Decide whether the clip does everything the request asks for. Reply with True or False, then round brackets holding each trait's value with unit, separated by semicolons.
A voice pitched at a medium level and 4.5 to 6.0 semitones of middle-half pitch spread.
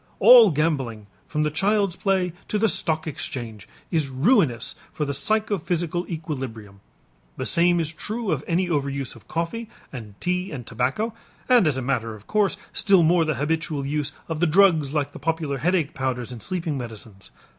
True (155 Hz; 5.3 semitones)